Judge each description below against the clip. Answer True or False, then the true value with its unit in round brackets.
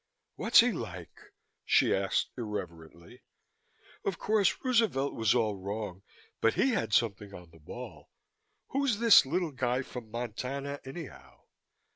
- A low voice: True (120 Hz)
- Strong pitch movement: True (8.3 semitones)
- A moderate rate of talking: False (130 wpm)